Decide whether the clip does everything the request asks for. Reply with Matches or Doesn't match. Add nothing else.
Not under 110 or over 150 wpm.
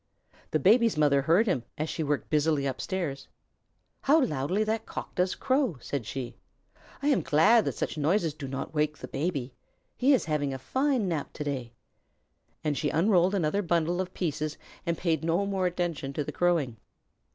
Doesn't match